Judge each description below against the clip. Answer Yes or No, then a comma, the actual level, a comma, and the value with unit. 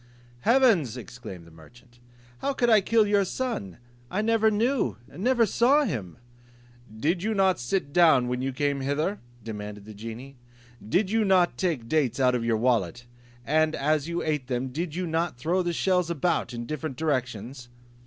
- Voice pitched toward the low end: No, medium, 150 Hz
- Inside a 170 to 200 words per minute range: Yes, average, 175 wpm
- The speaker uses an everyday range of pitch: No, wide, 7.7 semitones